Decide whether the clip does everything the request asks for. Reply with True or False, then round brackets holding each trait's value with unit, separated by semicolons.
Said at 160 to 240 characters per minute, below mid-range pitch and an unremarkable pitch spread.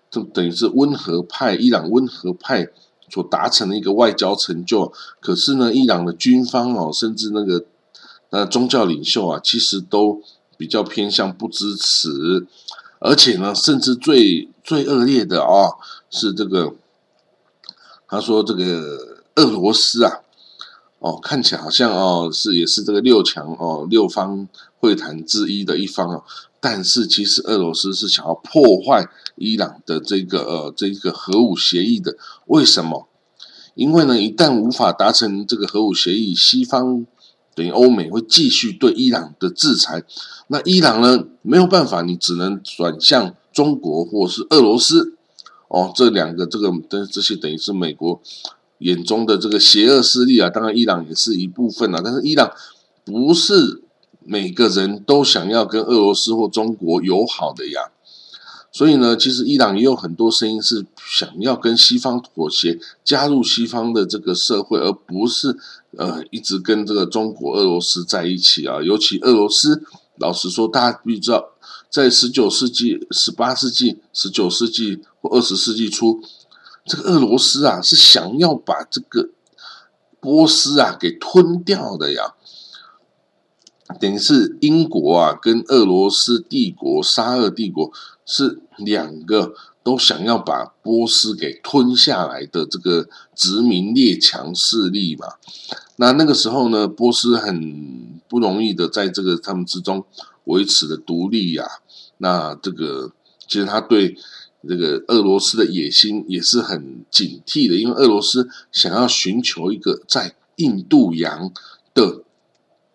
True (230 characters per minute; 115 Hz; 4.8 semitones)